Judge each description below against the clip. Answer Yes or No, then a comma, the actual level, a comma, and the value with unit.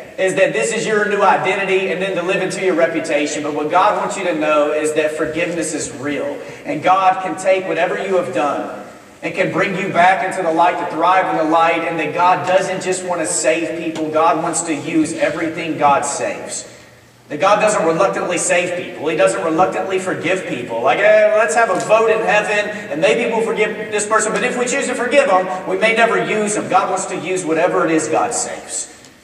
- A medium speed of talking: No, fast, 225 wpm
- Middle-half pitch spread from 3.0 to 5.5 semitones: Yes, average, 3.7 semitones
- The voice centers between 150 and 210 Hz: Yes, medium, 185 Hz